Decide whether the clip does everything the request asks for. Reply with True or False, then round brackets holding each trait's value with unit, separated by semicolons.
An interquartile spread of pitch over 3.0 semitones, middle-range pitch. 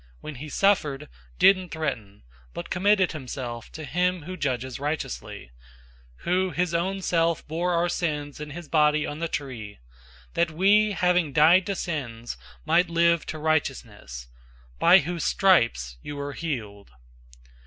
True (4.6 semitones; 155 Hz)